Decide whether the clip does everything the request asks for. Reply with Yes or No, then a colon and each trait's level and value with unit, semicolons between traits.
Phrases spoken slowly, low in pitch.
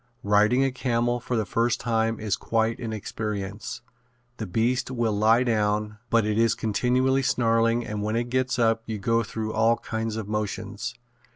No: average, 175 wpm; low, 115 Hz